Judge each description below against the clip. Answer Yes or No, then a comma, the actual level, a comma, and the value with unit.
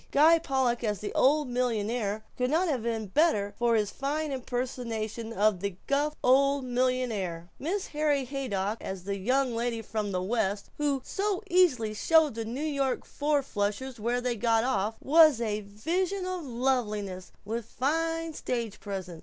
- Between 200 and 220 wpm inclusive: No, average, 165 wpm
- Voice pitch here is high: Yes, high, 245 Hz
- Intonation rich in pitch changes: No, average, 5.0 semitones